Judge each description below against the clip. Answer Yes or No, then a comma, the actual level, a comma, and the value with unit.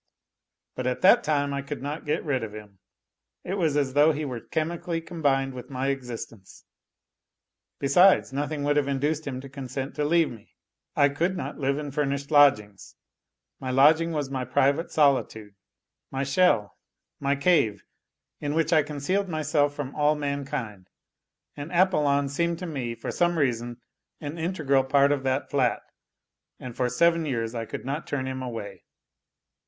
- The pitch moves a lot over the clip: No, average, 3.0 semitones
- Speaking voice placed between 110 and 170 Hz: Yes, medium, 140 Hz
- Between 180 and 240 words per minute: No, average, 165 wpm